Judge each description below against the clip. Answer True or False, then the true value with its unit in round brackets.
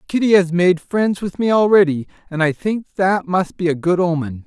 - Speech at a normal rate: False (215 wpm)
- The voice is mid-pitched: True (180 Hz)